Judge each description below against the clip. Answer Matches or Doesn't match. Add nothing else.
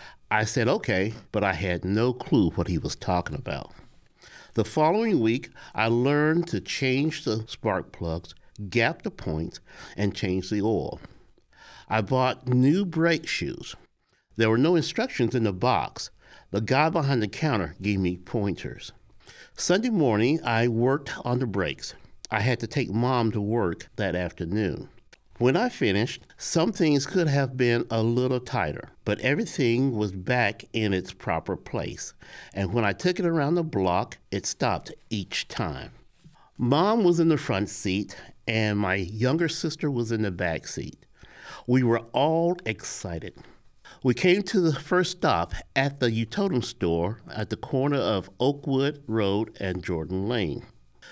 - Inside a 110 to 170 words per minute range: Matches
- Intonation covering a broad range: Matches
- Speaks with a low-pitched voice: Matches